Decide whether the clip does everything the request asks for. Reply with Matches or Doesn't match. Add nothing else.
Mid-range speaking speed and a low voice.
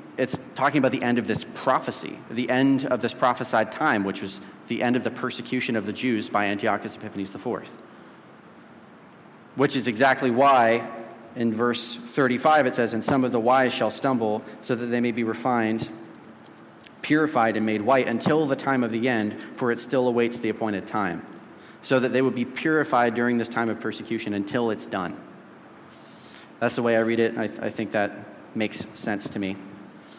Matches